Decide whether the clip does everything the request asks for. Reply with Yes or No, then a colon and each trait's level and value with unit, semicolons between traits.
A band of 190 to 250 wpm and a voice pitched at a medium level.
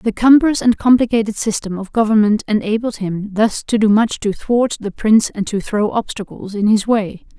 No: average, 195 wpm; high, 215 Hz